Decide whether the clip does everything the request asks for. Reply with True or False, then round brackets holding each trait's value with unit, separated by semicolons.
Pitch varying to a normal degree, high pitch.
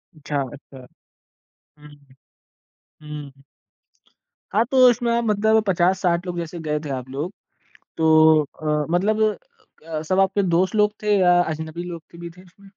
False (4.0 semitones; 170 Hz)